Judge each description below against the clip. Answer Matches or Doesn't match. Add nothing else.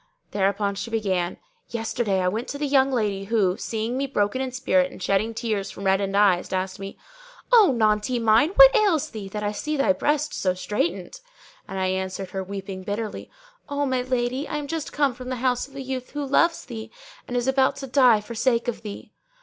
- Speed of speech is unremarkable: Doesn't match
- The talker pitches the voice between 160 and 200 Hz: Doesn't match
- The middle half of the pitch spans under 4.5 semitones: Doesn't match